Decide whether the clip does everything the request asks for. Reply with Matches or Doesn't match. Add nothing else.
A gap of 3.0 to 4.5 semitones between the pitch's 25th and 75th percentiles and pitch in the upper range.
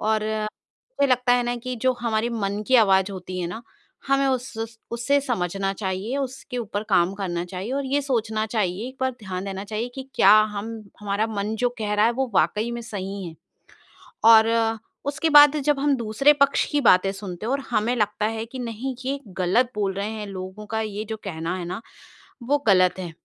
Matches